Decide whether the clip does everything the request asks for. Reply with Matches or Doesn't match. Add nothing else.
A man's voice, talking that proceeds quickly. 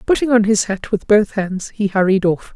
Doesn't match